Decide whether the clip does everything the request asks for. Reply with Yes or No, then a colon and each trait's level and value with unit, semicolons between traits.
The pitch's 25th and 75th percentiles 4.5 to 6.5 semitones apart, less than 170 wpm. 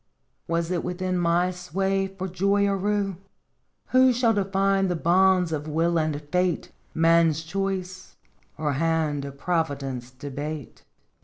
No: average, 3.5 semitones; slow, 135 wpm